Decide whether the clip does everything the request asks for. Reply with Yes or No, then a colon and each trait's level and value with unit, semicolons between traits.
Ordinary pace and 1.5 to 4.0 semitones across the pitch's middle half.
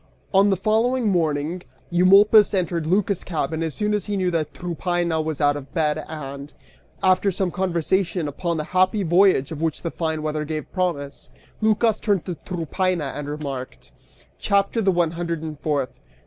Yes: average, 170 wpm; average, 3.7 semitones